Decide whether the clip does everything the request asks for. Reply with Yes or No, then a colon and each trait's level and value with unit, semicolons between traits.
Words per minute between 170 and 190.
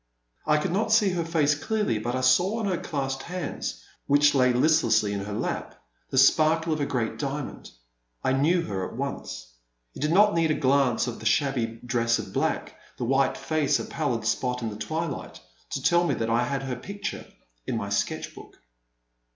No: average, 200 wpm